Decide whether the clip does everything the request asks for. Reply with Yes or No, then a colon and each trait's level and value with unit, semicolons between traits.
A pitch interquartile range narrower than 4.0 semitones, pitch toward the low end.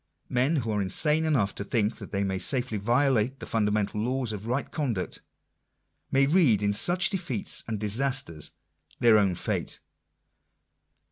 No: average, 4.8 semitones; low, 115 Hz